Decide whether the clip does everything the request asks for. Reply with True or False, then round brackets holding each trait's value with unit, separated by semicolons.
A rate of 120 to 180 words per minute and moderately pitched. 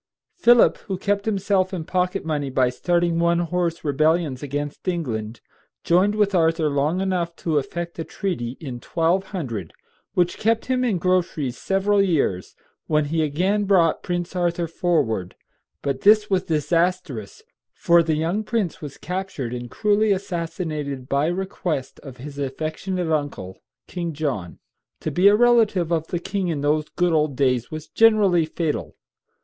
True (155 wpm; 170 Hz)